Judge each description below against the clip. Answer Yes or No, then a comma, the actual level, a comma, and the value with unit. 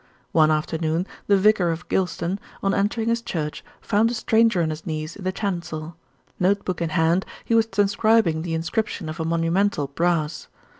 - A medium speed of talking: Yes, average, 180 wpm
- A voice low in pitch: No, medium, 175 Hz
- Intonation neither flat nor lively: Yes, average, 4.1 semitones